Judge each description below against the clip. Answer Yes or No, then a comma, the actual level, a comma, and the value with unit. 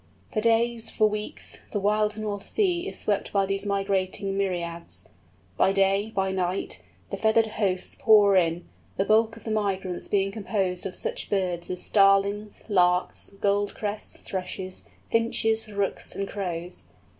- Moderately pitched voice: No, high, 200 Hz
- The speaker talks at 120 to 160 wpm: Yes, average, 145 wpm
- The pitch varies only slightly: Yes, narrow, 2.1 semitones